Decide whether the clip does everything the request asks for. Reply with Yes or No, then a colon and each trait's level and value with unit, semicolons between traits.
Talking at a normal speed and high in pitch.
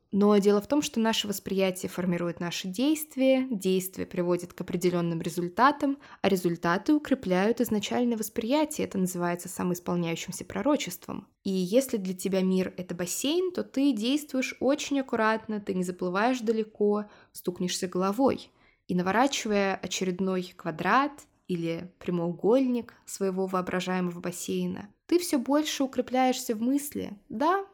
Yes: average, 125 wpm; high, 205 Hz